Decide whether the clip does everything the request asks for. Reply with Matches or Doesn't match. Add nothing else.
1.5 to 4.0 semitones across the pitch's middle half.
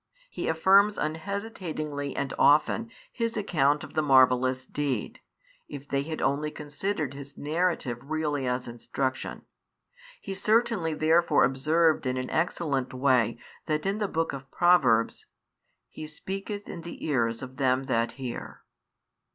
Doesn't match